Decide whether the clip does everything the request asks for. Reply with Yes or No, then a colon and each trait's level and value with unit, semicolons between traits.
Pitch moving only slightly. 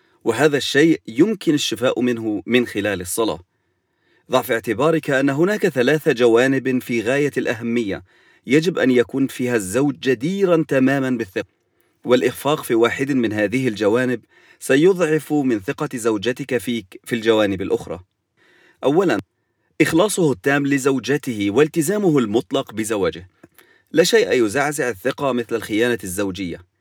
No: average, 4.2 semitones